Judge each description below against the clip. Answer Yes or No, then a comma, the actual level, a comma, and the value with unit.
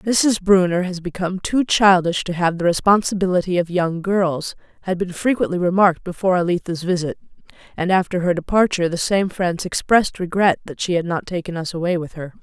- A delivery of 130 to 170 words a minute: No, average, 185 wpm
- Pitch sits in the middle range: Yes, medium, 180 Hz